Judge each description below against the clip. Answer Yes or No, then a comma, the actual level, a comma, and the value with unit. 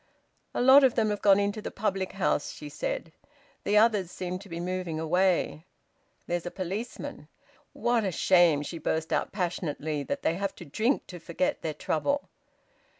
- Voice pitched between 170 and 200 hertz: Yes, medium, 185 Hz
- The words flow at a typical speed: Yes, average, 175 wpm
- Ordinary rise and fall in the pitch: Yes, average, 3.9 semitones